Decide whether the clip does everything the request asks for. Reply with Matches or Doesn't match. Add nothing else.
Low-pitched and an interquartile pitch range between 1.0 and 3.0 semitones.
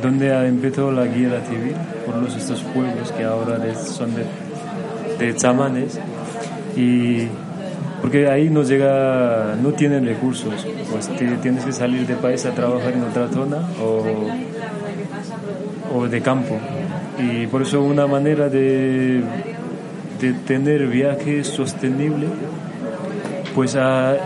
Matches